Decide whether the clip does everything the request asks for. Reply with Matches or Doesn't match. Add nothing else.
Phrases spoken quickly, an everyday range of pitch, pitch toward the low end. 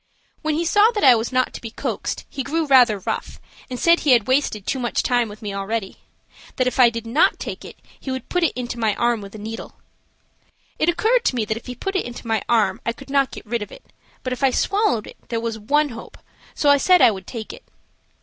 Doesn't match